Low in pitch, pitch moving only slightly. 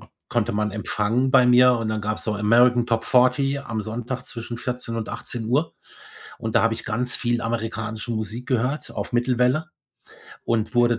Yes: low, 120 Hz; narrow, 2.1 semitones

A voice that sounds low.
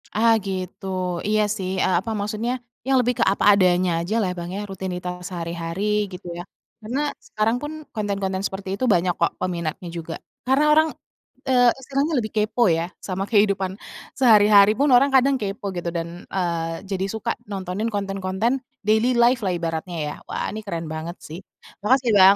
No: high, 195 Hz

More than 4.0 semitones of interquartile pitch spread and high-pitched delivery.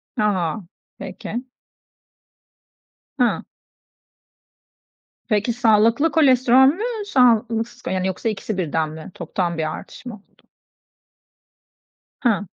Yes: average, 5.0 semitones; high, 225 Hz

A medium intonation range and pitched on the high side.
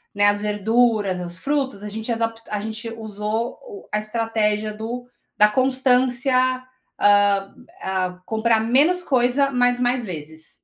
Yes: average, 3.1 semitones; high, 225 Hz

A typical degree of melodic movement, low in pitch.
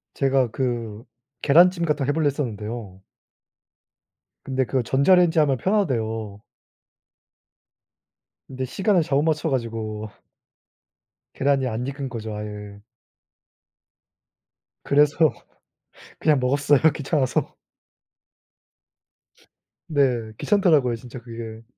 Yes: average, 4.6 semitones; low, 130 Hz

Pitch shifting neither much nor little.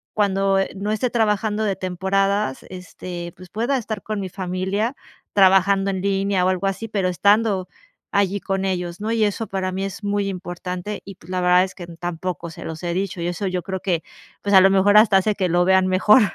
No: narrow, 1.9 semitones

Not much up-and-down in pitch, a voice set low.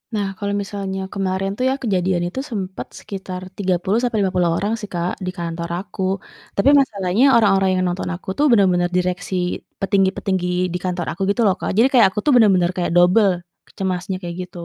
No: narrow, 2.0 semitones; high, 190 Hz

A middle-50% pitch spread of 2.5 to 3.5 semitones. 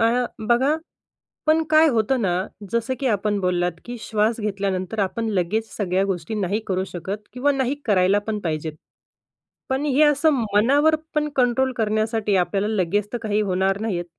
No: average, 4.5 semitones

